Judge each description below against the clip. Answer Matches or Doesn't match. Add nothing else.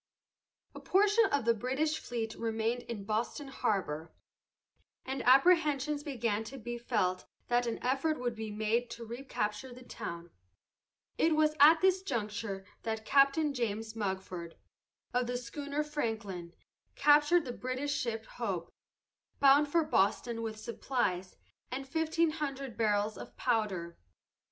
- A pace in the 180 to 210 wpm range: Doesn't match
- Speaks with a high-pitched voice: Matches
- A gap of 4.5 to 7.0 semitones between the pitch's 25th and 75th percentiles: Matches